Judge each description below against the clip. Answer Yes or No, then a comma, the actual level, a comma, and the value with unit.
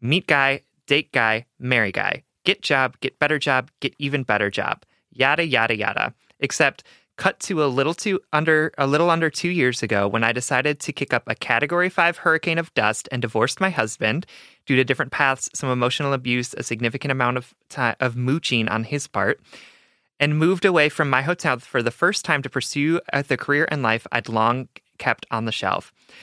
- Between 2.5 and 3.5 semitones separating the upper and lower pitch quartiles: No, average, 4.1 semitones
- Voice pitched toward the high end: No, low, 135 Hz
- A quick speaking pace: No, average, 195 wpm